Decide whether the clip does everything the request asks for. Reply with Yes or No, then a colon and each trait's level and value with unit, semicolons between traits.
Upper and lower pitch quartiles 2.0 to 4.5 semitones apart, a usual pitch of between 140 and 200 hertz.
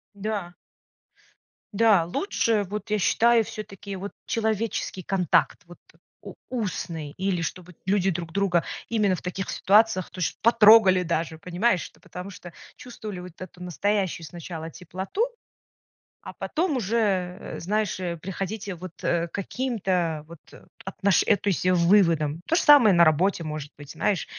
Yes: average, 3.5 semitones; high, 190 Hz